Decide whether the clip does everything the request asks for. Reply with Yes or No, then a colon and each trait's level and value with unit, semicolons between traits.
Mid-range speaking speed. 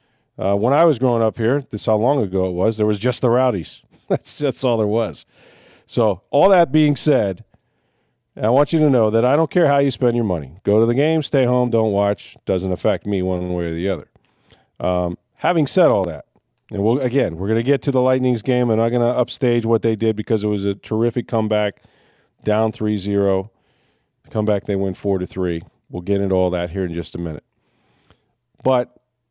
No: fast, 225 wpm